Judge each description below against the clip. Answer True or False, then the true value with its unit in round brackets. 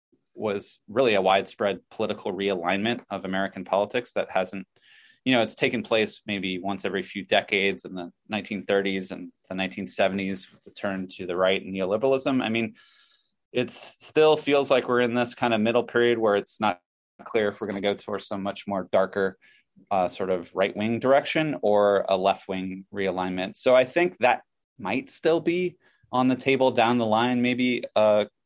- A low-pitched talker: True (105 Hz)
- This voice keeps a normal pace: True (185 wpm)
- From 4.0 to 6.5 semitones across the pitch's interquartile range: True (4.5 semitones)